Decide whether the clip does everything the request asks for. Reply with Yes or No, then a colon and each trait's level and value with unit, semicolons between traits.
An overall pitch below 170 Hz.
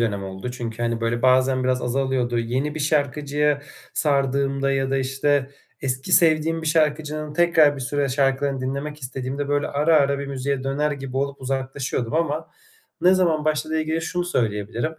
Yes: medium, 140 Hz